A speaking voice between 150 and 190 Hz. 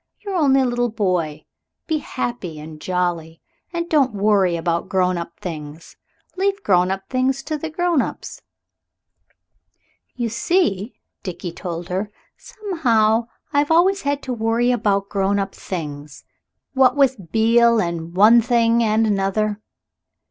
No: high, 220 Hz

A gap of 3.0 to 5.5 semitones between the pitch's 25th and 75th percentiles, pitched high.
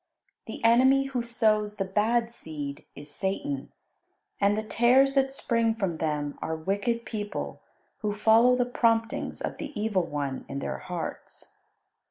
Yes: average, 4.4 semitones; high, 215 Hz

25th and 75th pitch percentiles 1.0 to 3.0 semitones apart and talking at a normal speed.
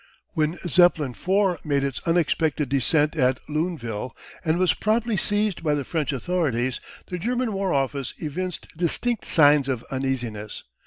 No: average, 5.1 semitones; average, 145 wpm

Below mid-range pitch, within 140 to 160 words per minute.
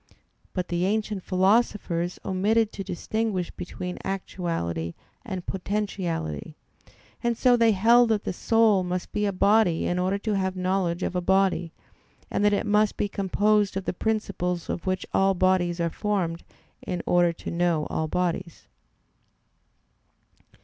No: high, 190 Hz; average, 150 wpm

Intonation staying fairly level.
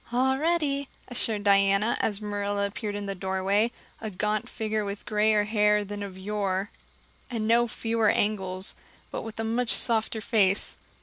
Yes: narrow, 2.0 semitones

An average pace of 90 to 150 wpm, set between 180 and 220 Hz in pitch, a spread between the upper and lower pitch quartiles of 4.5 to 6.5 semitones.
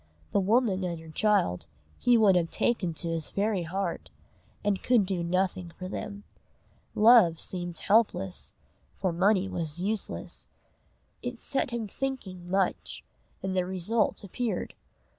No: average, 140 wpm; high, 190 Hz; average, 3.6 semitones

